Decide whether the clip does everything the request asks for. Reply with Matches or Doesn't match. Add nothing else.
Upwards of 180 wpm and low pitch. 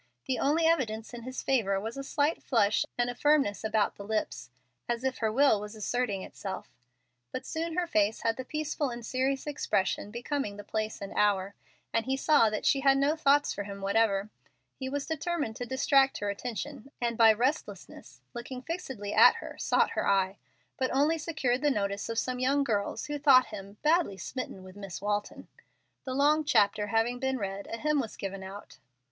Doesn't match